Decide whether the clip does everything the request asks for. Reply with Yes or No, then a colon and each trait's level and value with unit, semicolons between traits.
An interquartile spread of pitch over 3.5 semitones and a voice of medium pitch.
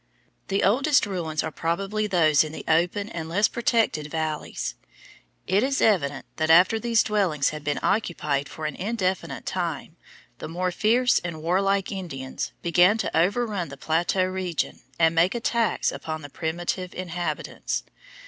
Yes: average, 4.4 semitones; medium, 180 Hz